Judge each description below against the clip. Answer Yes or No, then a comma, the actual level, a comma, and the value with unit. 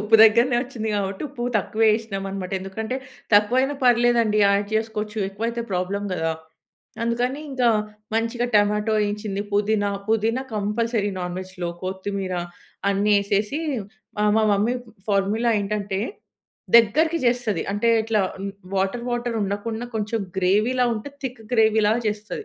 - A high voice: Yes, high, 215 Hz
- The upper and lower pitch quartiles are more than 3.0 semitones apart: No, average, 2.7 semitones